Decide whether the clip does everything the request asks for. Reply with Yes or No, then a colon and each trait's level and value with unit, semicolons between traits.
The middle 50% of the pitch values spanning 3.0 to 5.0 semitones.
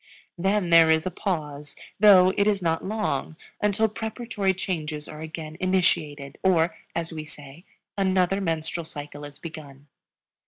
Yes: average, 3.8 semitones